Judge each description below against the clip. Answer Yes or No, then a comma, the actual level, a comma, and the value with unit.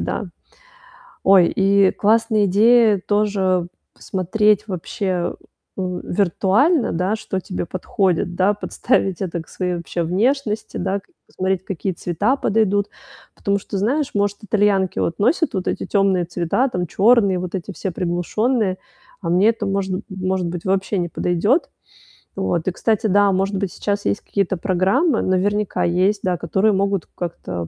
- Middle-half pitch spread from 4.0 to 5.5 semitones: No, narrow, 2.5 semitones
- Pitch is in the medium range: No, high, 195 Hz